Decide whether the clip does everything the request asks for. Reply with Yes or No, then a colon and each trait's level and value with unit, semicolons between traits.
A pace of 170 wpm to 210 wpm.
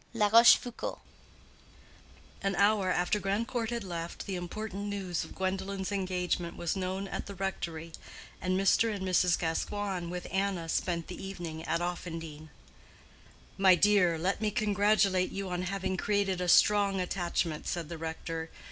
No: average, 145 wpm